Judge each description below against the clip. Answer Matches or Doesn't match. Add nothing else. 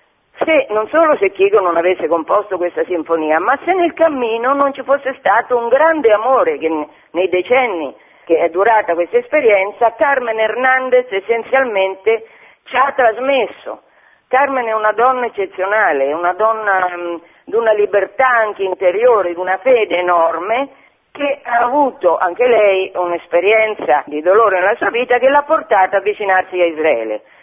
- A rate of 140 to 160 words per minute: Matches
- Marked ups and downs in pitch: Matches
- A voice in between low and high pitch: Doesn't match